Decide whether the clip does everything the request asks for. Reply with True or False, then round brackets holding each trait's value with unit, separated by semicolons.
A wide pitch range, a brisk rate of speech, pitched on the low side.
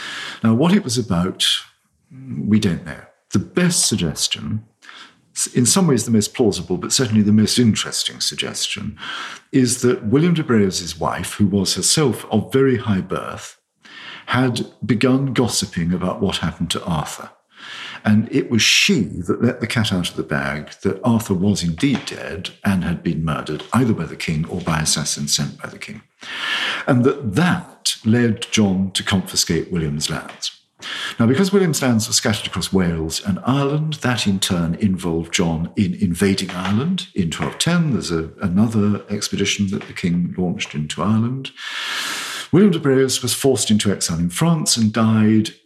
False (5.7 semitones; 165 wpm; 110 Hz)